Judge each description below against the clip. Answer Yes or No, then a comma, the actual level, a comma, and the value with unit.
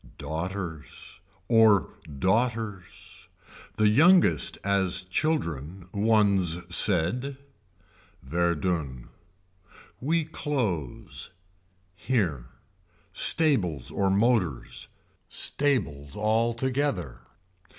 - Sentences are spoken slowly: Yes, slow, 60 wpm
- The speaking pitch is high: No, low, 100 Hz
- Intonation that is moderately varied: No, wide, 6.3 semitones